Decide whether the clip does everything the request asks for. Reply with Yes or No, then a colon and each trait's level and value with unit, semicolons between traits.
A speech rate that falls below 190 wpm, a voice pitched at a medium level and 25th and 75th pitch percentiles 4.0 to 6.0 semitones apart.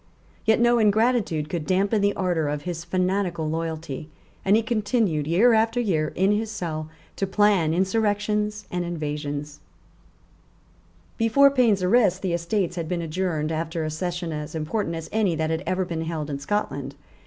Yes: average, 165 wpm; medium, 180 Hz; average, 4.7 semitones